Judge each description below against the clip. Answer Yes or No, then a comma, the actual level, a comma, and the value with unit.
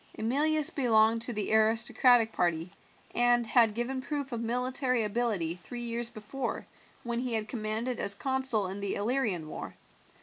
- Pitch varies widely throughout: No, average, 2.7 semitones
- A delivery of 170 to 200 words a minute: No, average, 155 wpm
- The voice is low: No, high, 235 Hz